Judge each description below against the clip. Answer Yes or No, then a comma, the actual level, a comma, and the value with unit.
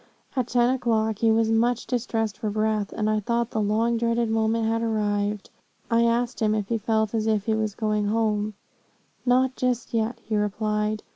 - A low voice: No, high, 220 Hz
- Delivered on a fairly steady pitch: Yes, narrow, 1.6 semitones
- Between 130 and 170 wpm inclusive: No, average, 190 wpm